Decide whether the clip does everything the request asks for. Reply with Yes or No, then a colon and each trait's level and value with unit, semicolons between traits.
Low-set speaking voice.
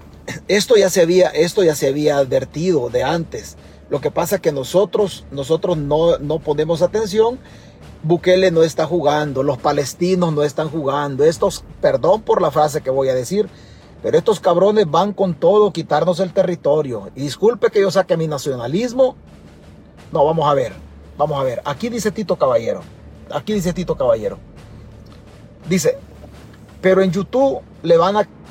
No: medium, 175 Hz